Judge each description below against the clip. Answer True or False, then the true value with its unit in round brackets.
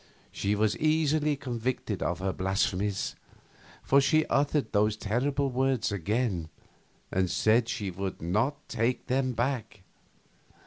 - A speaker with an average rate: False (125 wpm)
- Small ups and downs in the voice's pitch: False (5.2 semitones)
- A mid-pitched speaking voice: False (115 Hz)